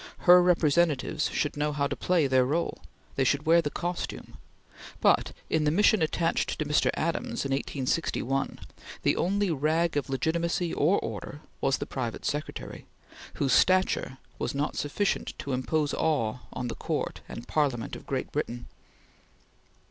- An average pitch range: Yes, average, 3.9 semitones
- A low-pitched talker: No, medium, 150 Hz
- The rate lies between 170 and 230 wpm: No, average, 155 wpm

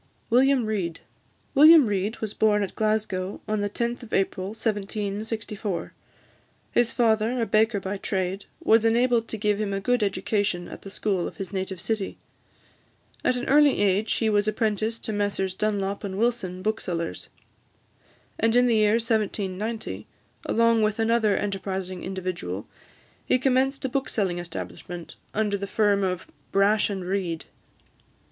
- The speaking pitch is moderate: No, high, 210 Hz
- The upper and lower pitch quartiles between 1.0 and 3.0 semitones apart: Yes, average, 2.7 semitones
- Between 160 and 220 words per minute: No, average, 150 wpm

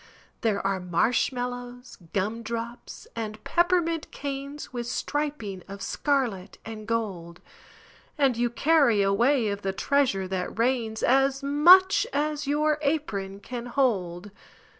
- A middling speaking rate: No, slow, 120 wpm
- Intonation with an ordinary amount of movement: No, wide, 5.7 semitones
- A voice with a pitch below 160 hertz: No, high, 240 Hz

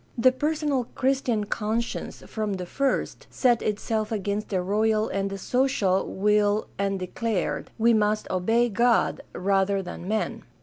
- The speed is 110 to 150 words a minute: Yes, average, 140 wpm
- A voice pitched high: Yes, high, 215 Hz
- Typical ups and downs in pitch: Yes, average, 3.0 semitones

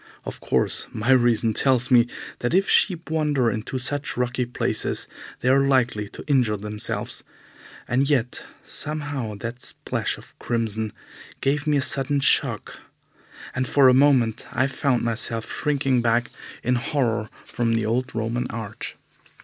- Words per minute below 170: Yes, average, 150 wpm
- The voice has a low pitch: Yes, low, 125 Hz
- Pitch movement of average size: Yes, average, 3.2 semitones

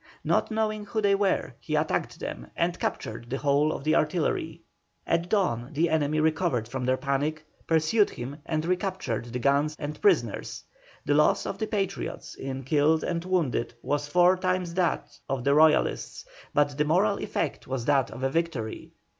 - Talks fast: No, average, 175 wpm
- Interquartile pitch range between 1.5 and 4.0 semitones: No, average, 4.7 semitones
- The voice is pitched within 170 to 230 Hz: No, medium, 155 Hz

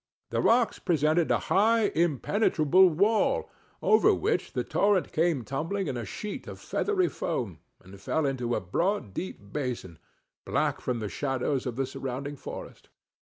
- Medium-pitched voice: Yes, medium, 150 Hz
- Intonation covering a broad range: Yes, wide, 7.5 semitones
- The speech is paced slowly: No, average, 155 wpm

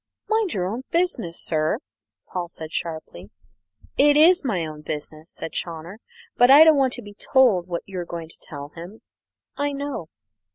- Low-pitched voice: No, medium, 185 Hz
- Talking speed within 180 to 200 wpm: No, average, 170 wpm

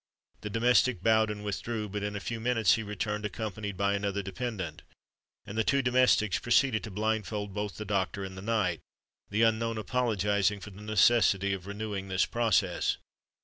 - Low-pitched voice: Yes, low, 105 Hz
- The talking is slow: No, average, 175 wpm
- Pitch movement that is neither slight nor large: No, narrow, 2.1 semitones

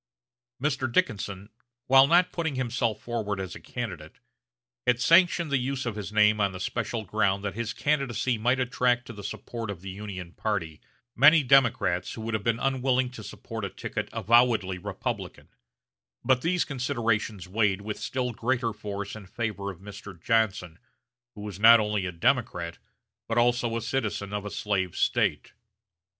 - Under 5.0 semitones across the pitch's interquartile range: Yes, average, 3.7 semitones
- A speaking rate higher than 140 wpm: Yes, average, 165 wpm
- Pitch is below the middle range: Yes, low, 110 Hz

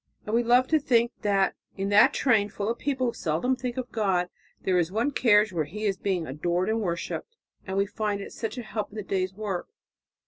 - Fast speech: Yes, fast, 230 wpm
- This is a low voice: No, high, 210 Hz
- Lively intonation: No, average, 3.8 semitones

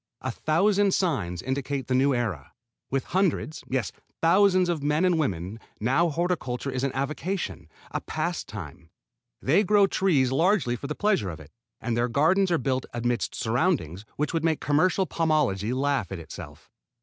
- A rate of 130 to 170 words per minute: Yes, average, 160 wpm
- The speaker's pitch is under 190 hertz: Yes, medium, 140 Hz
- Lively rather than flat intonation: Yes, wide, 6.2 semitones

